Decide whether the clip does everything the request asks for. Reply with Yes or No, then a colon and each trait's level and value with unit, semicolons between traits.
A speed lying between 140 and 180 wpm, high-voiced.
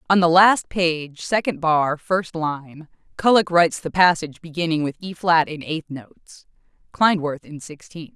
No: average, 160 wpm; medium, 165 Hz